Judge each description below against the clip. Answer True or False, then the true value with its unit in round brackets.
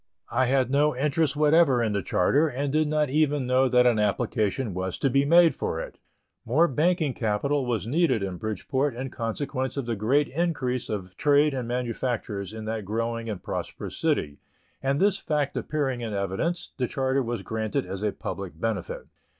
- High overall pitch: False (125 Hz)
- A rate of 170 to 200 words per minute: True (180 wpm)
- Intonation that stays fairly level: False (5.0 semitones)